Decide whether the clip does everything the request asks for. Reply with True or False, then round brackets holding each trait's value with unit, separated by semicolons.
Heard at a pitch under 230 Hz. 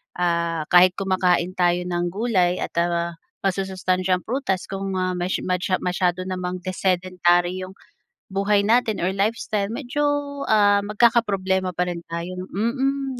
True (185 Hz)